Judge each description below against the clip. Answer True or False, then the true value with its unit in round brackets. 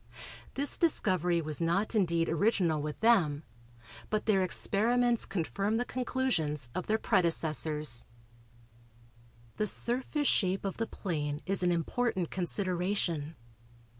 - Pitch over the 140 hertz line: True (185 Hz)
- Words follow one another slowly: True (115 wpm)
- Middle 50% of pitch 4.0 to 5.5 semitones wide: True (5.2 semitones)